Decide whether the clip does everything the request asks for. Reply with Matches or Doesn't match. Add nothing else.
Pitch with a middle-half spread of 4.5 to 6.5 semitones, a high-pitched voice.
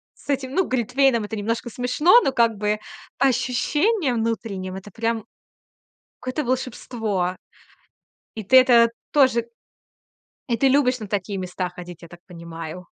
Matches